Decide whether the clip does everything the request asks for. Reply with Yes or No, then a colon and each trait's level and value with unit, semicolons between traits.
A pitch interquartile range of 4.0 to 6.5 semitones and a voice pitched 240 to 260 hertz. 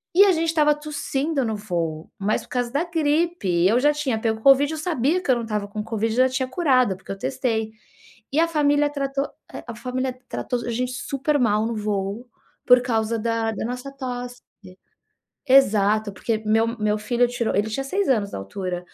Yes: average, 4.5 semitones; high, 245 Hz